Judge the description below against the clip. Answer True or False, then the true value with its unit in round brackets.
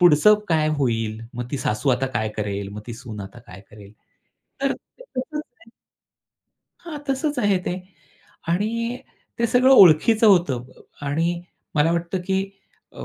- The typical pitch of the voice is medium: True (165 Hz)